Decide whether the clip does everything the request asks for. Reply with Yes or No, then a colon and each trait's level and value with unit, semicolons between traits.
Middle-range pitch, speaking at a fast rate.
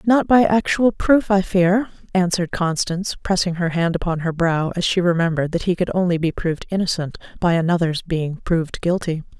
No: medium, 175 Hz; average, 185 wpm